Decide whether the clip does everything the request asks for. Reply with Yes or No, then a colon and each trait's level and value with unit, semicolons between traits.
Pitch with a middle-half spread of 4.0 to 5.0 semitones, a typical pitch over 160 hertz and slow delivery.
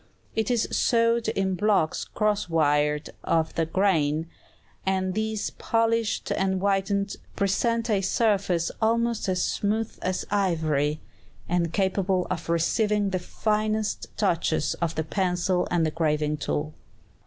Yes: average, 4.4 semitones; high, 190 Hz; slow, 125 wpm